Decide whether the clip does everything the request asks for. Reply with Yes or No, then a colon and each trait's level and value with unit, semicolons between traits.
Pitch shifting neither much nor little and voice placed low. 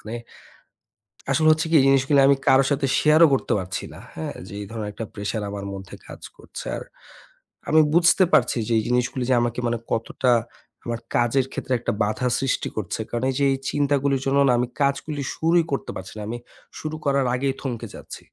Yes: average, 3.5 semitones; low, 130 Hz